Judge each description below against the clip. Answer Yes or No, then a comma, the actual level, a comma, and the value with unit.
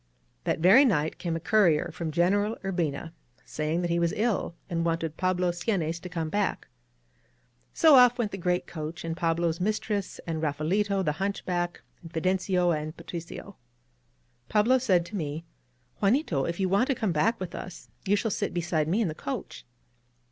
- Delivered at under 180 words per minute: No, average, 185 wpm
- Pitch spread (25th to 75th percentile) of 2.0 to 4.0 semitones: Yes, average, 3.5 semitones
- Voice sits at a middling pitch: Yes, medium, 175 Hz